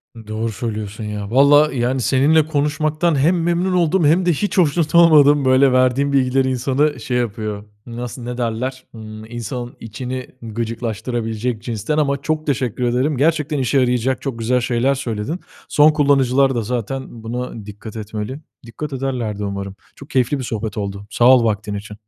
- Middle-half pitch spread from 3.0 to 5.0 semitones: Yes, average, 4.0 semitones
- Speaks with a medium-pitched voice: No, low, 125 Hz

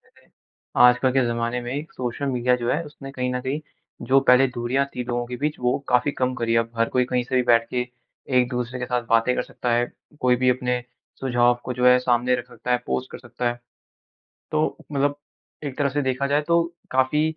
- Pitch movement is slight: Yes, narrow, 1.5 semitones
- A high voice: No, low, 125 Hz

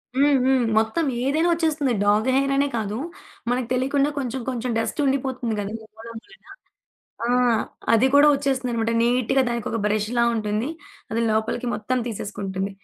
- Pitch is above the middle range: Yes, high, 245 Hz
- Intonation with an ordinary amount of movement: Yes, average, 3.7 semitones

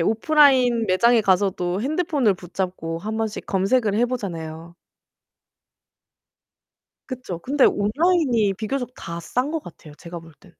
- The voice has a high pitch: Yes, high, 210 Hz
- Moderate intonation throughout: No, wide, 6.2 semitones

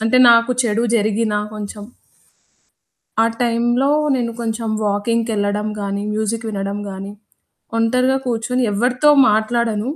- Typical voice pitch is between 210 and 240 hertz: Yes, high, 225 Hz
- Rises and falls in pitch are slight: Yes, narrow, 2.3 semitones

